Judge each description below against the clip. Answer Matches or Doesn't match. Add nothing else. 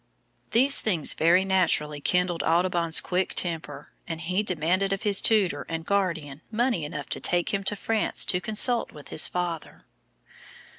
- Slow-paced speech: Doesn't match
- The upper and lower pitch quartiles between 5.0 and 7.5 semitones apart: Doesn't match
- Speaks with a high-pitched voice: Doesn't match